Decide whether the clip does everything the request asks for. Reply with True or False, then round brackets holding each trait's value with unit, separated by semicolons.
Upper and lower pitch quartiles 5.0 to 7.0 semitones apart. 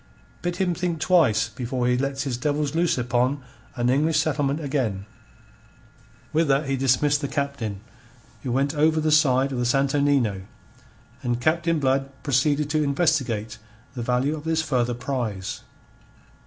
False (3.7 semitones)